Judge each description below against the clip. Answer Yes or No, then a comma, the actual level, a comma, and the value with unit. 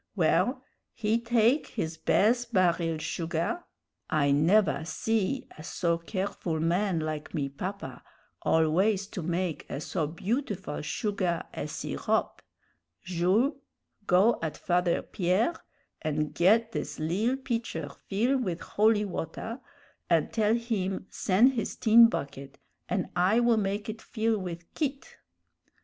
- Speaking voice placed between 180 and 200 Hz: Yes, high, 190 Hz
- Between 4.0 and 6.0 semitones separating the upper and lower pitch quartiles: Yes, average, 5.2 semitones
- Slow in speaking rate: Yes, slow, 130 wpm